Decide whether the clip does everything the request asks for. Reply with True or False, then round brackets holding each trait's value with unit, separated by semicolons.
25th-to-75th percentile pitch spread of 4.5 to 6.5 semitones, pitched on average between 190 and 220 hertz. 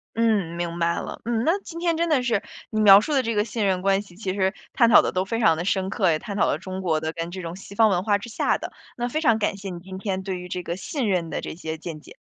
False (4.0 semitones; 195 Hz)